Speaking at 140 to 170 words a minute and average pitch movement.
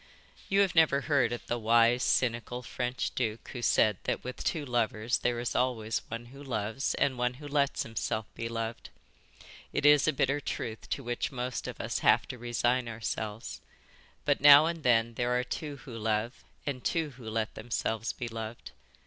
No: average, 185 wpm; average, 3.1 semitones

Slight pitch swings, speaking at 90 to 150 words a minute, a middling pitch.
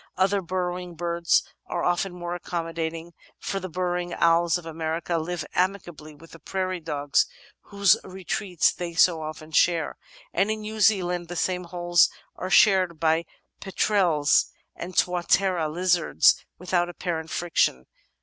Yes: narrow, 1.9 semitones; average, 140 wpm; medium, 175 Hz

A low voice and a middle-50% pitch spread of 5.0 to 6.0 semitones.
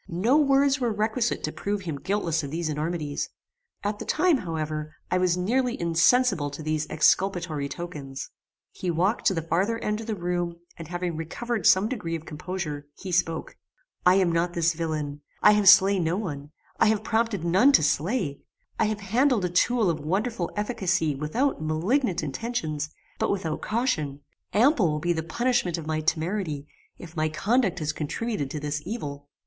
No: medium, 175 Hz; wide, 5.4 semitones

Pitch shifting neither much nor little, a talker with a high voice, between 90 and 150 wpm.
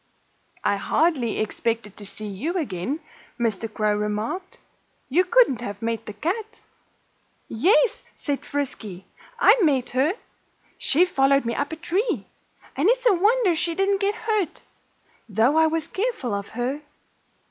No: wide, 8.9 semitones; very high, 285 Hz; average, 145 wpm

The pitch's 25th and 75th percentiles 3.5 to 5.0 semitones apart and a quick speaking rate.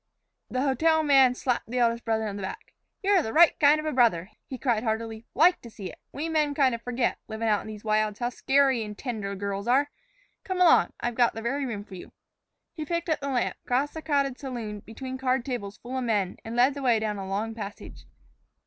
Yes: average, 4.2 semitones; fast, 230 wpm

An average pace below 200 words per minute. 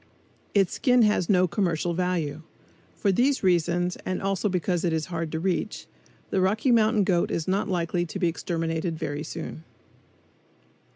Yes: average, 160 wpm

